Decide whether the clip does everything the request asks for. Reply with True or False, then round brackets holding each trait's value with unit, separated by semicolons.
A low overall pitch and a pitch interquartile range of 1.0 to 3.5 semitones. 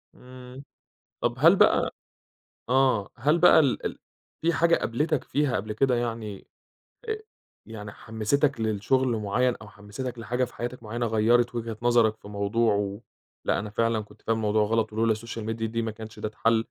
True (115 Hz; 2.8 semitones)